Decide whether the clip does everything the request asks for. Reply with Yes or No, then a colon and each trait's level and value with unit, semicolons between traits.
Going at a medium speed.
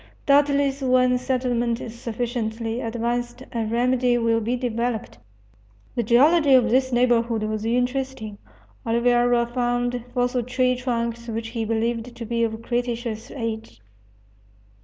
No: slow, 125 wpm